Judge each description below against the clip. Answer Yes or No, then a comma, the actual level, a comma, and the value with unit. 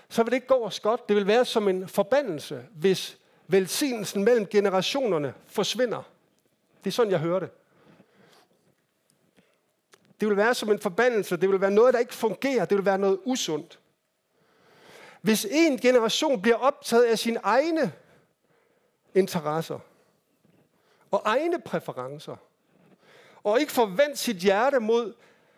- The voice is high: Yes, high, 220 Hz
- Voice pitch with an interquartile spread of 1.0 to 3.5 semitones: No, average, 4.7 semitones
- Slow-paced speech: Yes, slow, 140 wpm